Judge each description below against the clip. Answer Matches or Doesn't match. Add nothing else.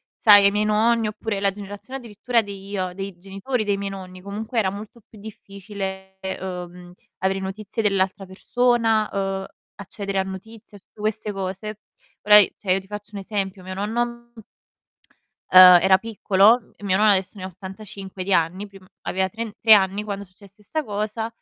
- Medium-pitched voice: Doesn't match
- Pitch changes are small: Matches